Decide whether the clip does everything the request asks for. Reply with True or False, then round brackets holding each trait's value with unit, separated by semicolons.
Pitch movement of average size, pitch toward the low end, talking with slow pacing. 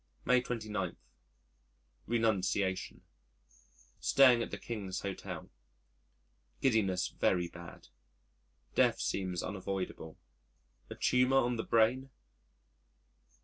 True (4.5 semitones; 110 Hz; 85 wpm)